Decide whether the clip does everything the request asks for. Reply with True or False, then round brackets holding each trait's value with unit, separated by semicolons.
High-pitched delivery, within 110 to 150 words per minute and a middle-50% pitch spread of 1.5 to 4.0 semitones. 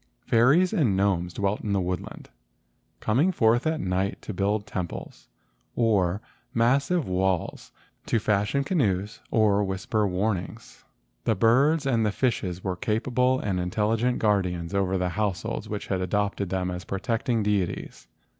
False (105 Hz; 145 wpm; 3.7 semitones)